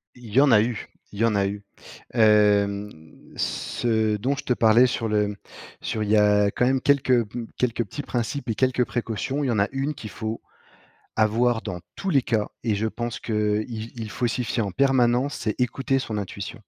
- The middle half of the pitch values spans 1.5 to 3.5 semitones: Yes, average, 2.9 semitones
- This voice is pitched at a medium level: No, low, 115 Hz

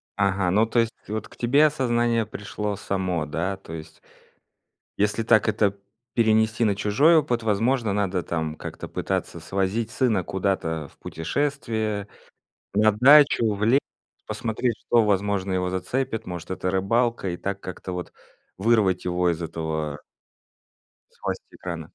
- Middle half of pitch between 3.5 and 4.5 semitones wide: Yes, average, 3.9 semitones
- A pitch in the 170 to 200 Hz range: No, low, 100 Hz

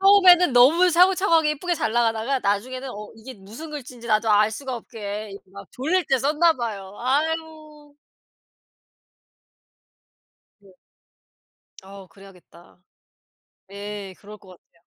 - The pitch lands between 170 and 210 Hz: No, high, 240 Hz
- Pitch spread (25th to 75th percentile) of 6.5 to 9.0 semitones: Yes, wide, 7.1 semitones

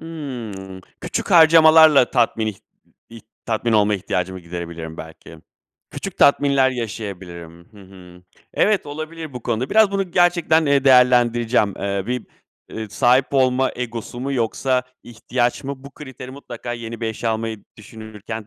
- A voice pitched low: Yes, low, 120 Hz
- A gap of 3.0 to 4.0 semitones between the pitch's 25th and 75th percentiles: No, average, 4.7 semitones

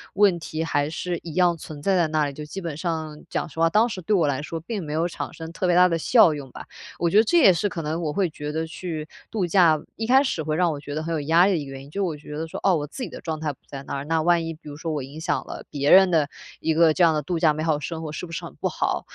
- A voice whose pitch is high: No, medium, 160 Hz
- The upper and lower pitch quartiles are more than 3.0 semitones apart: No, average, 2.7 semitones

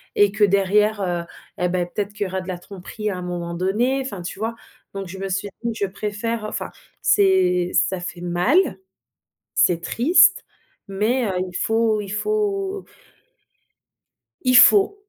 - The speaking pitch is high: Yes, high, 200 Hz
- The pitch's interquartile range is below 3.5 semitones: No, average, 4.0 semitones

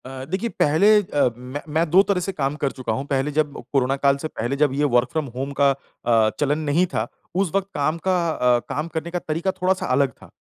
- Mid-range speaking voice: Yes, medium, 145 Hz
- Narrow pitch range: No, average, 3.8 semitones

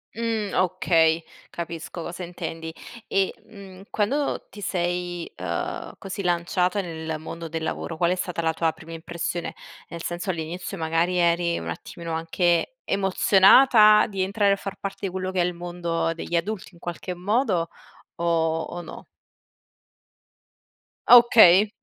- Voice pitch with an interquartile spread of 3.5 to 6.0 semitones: No, narrow, 2.6 semitones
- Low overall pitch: No, medium, 175 Hz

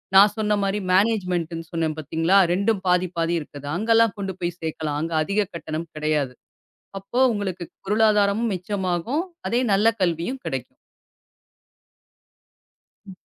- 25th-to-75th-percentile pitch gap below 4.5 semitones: Yes, average, 4.1 semitones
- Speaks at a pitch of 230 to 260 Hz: No, medium, 185 Hz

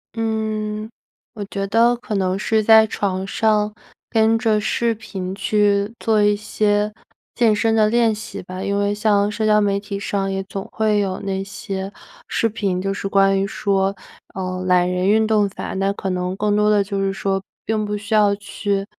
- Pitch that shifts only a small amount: Yes, narrow, 1.7 semitones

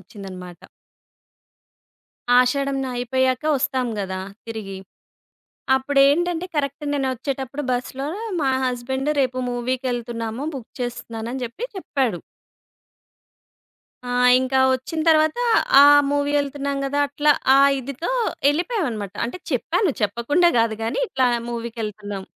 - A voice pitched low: No, very high, 260 Hz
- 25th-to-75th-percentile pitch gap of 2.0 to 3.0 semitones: No, average, 3.5 semitones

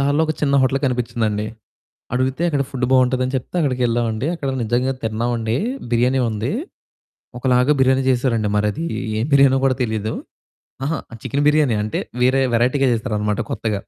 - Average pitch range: Yes, average, 3.1 semitones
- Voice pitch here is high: No, low, 125 Hz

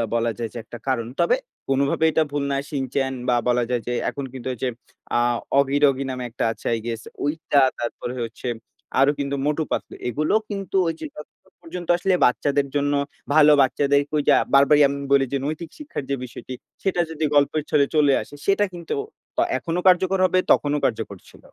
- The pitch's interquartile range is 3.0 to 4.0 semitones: Yes, average, 3.6 semitones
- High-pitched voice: No, medium, 140 Hz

